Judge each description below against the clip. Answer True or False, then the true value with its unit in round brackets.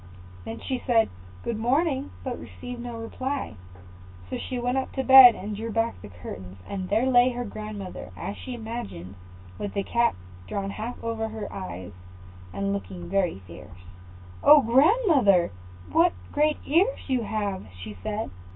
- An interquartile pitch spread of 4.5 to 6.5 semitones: True (5.2 semitones)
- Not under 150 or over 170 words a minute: True (160 wpm)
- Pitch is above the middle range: True (225 Hz)